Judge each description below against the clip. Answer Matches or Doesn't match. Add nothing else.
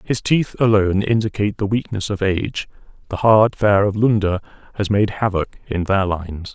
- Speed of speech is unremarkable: Matches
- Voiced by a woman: Doesn't match